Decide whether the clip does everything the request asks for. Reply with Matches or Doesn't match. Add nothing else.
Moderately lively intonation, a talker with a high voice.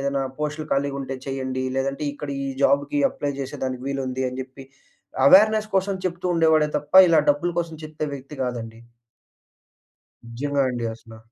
Doesn't match